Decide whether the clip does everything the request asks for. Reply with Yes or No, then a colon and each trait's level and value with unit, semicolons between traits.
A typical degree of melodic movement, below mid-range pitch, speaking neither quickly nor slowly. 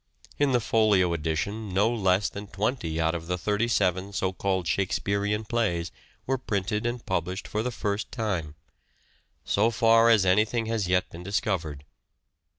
Yes: average, 3.6 semitones; low, 100 Hz; average, 160 wpm